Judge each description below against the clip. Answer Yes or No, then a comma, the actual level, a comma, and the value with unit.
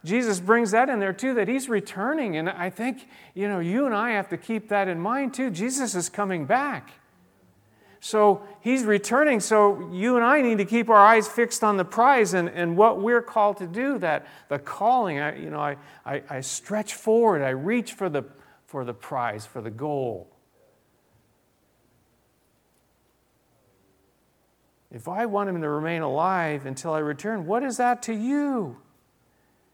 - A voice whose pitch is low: No, high, 205 Hz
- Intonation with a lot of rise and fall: Yes, wide, 6.3 semitones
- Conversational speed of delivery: Yes, average, 175 wpm